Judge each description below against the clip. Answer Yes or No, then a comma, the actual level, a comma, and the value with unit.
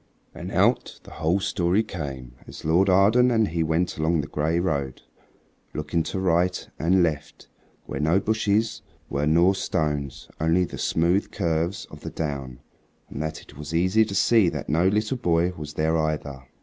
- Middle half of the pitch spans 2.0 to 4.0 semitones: Yes, average, 3.7 semitones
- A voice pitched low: Yes, very low, 85 Hz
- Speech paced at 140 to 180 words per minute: Yes, average, 175 wpm